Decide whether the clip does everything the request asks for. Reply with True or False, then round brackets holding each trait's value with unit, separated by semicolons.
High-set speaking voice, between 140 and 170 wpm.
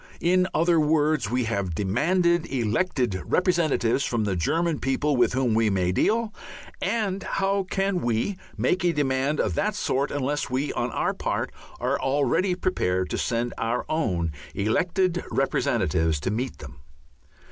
False (140 Hz; 150 wpm)